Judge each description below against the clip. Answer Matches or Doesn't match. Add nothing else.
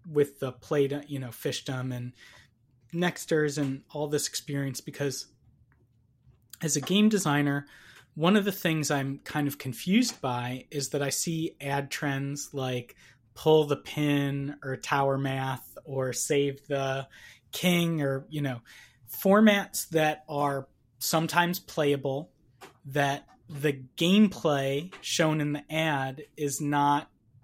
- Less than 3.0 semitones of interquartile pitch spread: Matches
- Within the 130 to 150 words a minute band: Matches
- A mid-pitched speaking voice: Matches